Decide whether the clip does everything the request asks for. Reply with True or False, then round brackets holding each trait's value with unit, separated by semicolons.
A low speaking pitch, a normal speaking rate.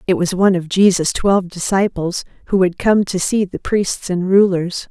False (185 Hz; 195 wpm)